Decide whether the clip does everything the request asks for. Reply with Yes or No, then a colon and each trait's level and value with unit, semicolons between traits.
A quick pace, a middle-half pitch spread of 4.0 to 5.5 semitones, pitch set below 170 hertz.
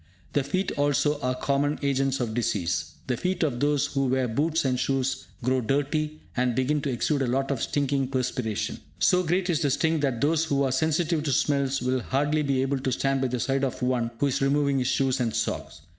No: fast, 220 wpm; narrow, 2.4 semitones; low, 135 Hz